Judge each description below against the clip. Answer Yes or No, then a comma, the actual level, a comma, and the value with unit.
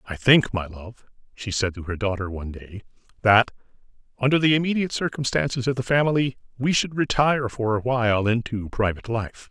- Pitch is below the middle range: Yes, low, 115 Hz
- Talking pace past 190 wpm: No, average, 175 wpm